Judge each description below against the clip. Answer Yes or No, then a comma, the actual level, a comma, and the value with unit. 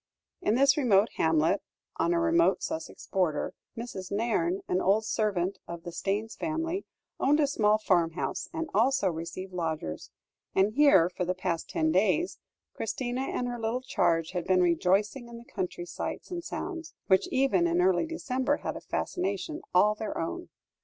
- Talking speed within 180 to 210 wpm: No, average, 165 wpm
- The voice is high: Yes, high, 210 Hz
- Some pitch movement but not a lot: No, wide, 7.1 semitones